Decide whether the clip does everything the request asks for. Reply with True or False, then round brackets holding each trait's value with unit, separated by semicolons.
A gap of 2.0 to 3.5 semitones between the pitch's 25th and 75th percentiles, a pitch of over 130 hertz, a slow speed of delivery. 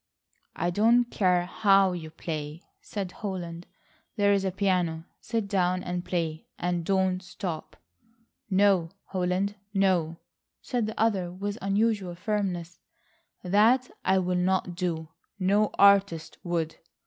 True (2.4 semitones; 185 Hz; 125 wpm)